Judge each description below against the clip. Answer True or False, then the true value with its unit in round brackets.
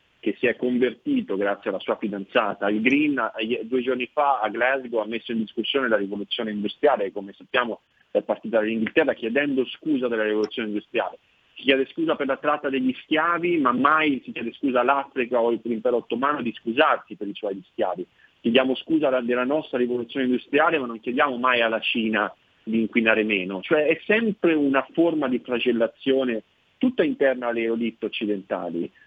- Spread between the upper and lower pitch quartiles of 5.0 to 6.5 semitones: False (3.9 semitones)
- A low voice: True (125 Hz)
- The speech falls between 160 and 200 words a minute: True (170 wpm)